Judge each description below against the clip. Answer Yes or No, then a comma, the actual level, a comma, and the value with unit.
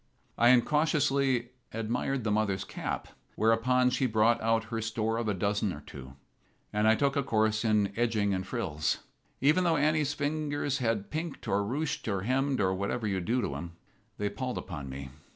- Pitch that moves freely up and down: No, average, 4.8 semitones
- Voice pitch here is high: No, low, 115 Hz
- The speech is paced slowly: No, average, 180 wpm